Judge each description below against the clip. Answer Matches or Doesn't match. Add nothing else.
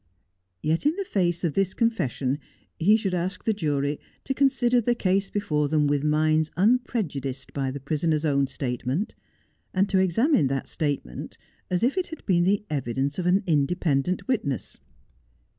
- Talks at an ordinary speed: Matches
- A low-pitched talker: Doesn't match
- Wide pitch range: Matches